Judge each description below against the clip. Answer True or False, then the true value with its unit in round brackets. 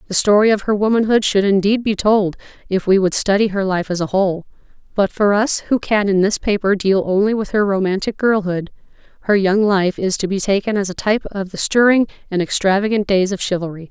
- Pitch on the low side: False (200 Hz)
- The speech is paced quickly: True (215 wpm)